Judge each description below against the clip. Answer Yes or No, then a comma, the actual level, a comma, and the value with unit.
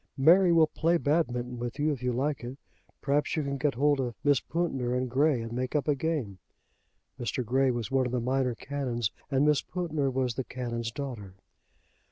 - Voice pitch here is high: No, low, 135 Hz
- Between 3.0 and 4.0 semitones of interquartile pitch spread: Yes, average, 3.3 semitones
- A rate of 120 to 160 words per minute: No, average, 200 wpm